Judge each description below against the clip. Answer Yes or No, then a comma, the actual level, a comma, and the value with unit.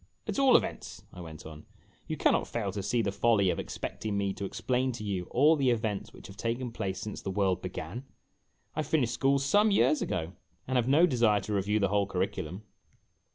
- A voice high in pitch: No, low, 105 Hz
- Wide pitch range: No, average, 4.6 semitones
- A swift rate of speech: Yes, fast, 210 wpm